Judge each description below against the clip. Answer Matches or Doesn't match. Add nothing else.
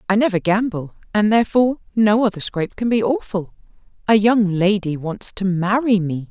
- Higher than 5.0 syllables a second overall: Matches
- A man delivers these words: Doesn't match